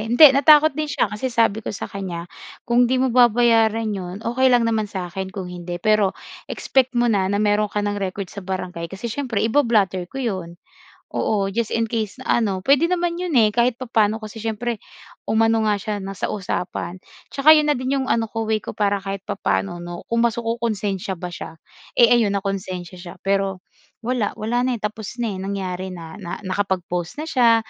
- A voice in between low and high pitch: No, high, 215 Hz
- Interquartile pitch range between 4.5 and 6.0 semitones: No, average, 3.7 semitones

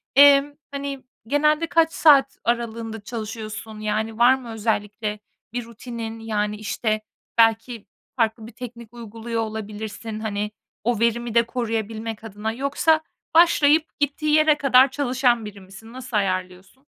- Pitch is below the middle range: No, high, 230 Hz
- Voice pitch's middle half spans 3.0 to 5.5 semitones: Yes, average, 3.3 semitones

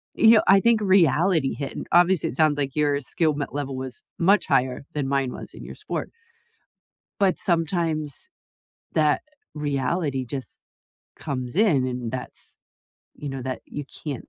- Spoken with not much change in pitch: No, average, 4.3 semitones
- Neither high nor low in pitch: Yes, medium, 145 Hz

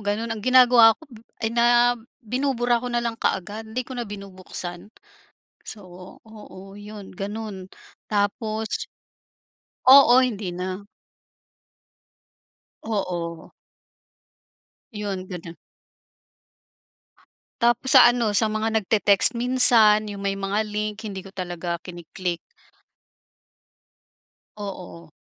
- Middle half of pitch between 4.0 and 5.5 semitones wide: No, average, 3.5 semitones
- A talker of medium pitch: No, high, 210 Hz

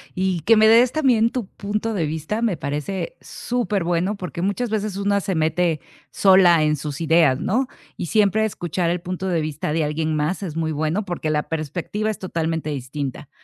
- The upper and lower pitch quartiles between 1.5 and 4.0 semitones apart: No, average, 4.9 semitones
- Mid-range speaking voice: Yes, medium, 175 Hz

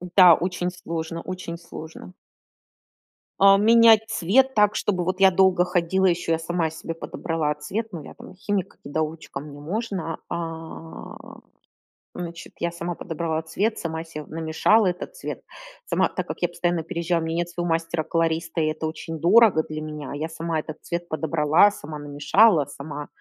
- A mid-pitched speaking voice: Yes, medium, 165 Hz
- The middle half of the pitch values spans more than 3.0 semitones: No, narrow, 2.4 semitones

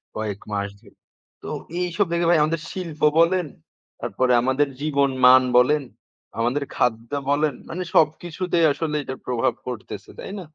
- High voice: No, medium, 145 Hz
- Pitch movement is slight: No, average, 5.0 semitones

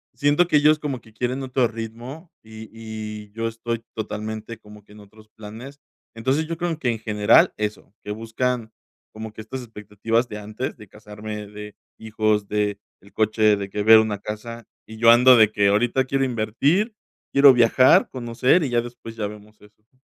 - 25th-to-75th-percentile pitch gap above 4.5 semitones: No, average, 2.9 semitones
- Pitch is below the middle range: Yes, low, 110 Hz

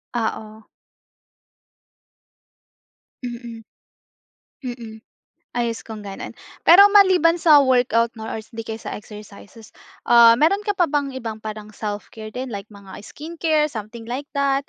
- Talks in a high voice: Yes, high, 230 Hz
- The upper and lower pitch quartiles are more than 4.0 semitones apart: Yes, average, 4.4 semitones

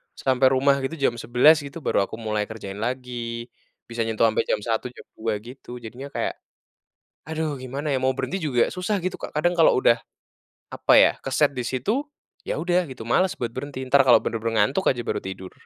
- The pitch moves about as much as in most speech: Yes, average, 3.8 semitones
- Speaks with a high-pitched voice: No, low, 130 Hz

